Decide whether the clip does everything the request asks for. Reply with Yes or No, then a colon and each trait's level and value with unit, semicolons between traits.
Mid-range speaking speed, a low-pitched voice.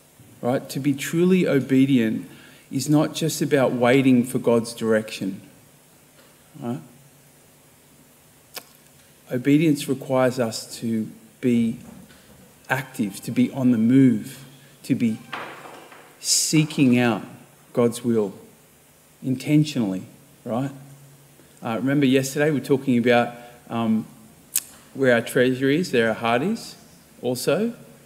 No: slow, 105 wpm; low, 130 Hz